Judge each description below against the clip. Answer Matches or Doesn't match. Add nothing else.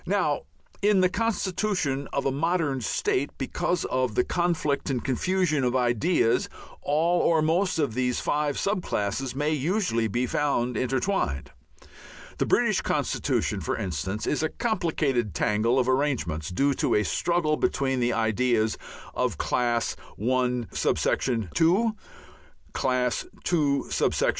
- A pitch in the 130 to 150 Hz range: Matches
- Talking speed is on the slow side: Matches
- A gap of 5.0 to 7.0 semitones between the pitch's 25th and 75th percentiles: Matches